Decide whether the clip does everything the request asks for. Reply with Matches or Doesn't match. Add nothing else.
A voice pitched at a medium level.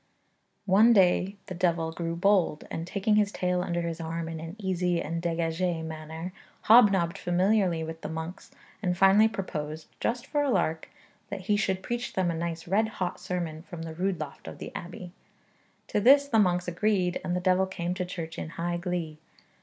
Matches